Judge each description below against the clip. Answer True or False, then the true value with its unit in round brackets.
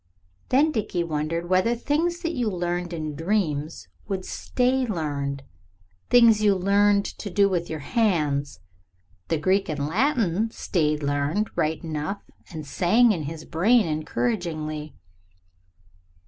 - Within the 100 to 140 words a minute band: True (135 wpm)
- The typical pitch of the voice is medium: True (175 Hz)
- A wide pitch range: True (5.8 semitones)